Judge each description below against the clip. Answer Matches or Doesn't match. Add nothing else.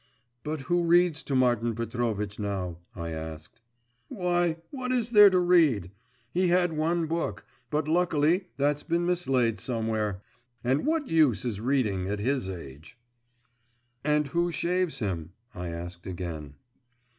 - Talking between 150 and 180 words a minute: Doesn't match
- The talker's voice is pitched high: Doesn't match